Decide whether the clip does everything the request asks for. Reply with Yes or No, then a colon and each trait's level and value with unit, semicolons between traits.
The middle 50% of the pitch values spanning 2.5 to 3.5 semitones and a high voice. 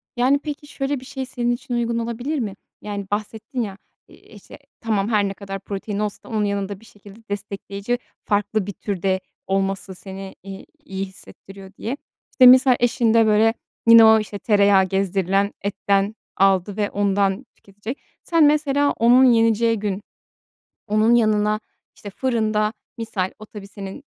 Yes: average, 3.1 semitones; high, 210 Hz